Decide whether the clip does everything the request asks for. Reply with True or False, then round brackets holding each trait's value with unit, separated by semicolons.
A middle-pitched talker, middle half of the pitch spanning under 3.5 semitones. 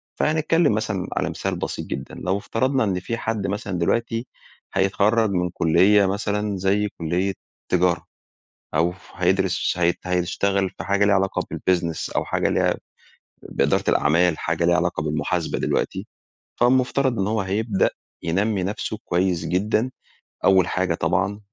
False (95 Hz; 3.1 semitones)